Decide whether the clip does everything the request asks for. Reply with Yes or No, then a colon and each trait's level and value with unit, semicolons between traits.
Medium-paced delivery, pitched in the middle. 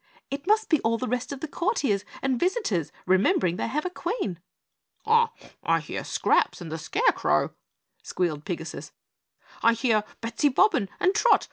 No: average, 155 wpm; very high, 250 Hz